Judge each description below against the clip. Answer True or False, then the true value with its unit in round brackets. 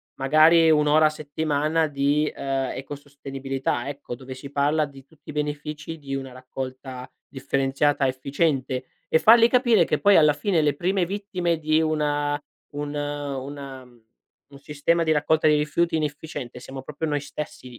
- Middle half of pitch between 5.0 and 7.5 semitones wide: False (2.4 semitones)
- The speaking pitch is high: False (145 Hz)